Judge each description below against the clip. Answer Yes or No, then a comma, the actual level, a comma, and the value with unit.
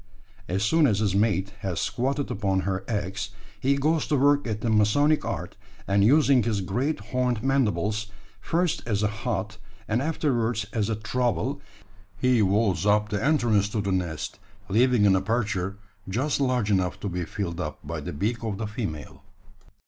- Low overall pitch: Yes, low, 110 Hz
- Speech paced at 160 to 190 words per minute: Yes, average, 170 wpm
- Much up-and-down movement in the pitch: No, average, 4.2 semitones